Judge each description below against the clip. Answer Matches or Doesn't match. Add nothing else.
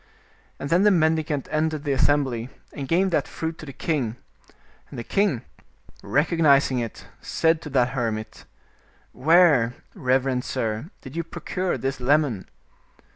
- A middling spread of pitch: Matches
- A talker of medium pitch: Matches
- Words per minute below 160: Matches